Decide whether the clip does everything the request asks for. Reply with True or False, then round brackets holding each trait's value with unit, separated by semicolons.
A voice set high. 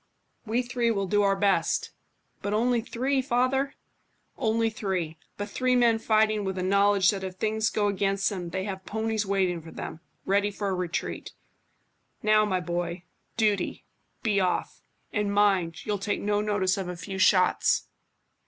True (205 Hz)